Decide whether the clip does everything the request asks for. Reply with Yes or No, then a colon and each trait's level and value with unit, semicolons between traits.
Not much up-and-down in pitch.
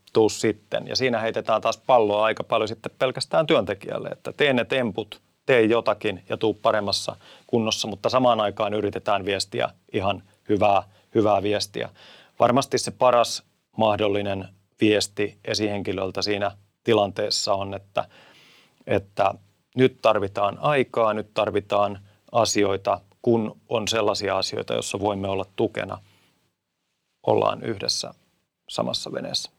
Yes: narrow, 1.8 semitones